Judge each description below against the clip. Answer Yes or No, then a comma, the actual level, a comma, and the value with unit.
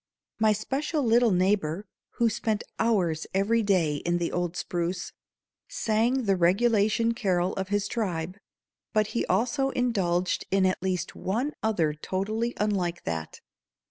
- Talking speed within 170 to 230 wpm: No, average, 140 wpm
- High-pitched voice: Yes, high, 200 Hz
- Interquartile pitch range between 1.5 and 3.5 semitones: No, average, 4.4 semitones